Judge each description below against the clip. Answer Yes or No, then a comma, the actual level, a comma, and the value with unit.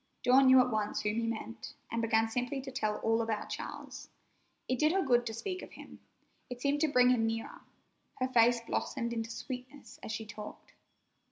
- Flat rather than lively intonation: Yes, narrow, 2.3 semitones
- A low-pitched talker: No, high, 240 Hz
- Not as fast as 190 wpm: No, average, 195 wpm